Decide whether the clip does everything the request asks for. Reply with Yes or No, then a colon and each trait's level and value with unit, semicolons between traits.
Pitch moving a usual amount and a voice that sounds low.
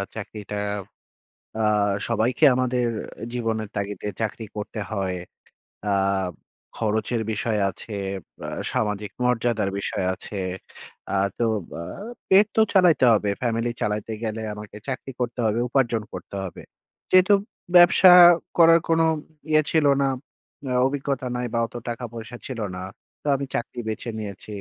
Yes: average, 3.5 semitones; low, 115 Hz